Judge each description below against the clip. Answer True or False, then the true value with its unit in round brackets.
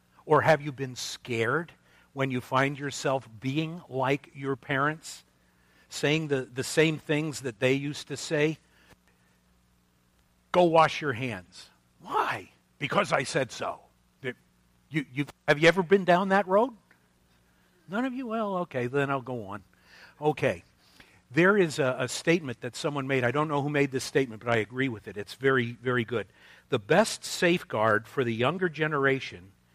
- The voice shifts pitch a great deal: True (7.0 semitones)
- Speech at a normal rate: True (165 wpm)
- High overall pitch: False (135 Hz)